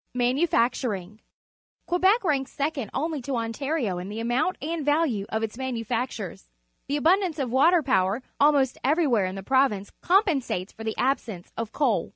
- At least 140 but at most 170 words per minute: Yes, average, 165 wpm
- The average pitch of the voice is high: Yes, very high, 260 Hz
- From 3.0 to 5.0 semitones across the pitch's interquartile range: No, wide, 5.4 semitones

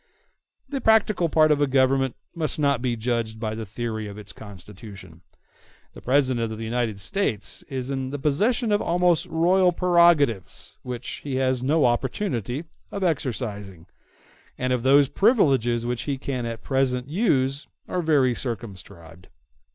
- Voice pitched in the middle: No, low, 130 Hz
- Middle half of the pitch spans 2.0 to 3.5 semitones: No, average, 5.3 semitones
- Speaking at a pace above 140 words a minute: Yes, average, 150 wpm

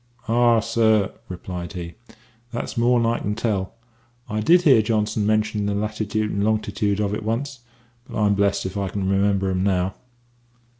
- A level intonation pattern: Yes, narrow, 2.1 semitones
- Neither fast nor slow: Yes, average, 165 wpm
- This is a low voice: Yes, low, 105 Hz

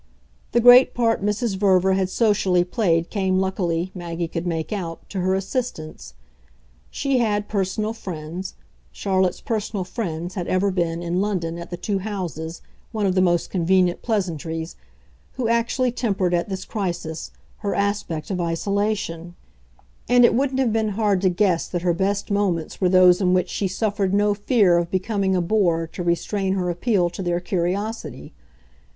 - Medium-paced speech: Yes, average, 165 wpm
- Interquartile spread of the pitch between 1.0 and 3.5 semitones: Yes, average, 3.1 semitones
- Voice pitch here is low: No, high, 190 Hz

